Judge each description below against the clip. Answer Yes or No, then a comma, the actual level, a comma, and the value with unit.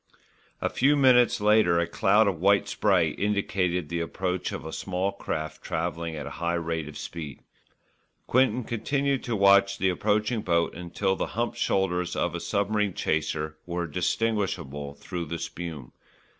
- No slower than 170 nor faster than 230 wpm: No, average, 155 wpm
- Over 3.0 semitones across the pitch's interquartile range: Yes, average, 3.9 semitones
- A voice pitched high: No, very low, 90 Hz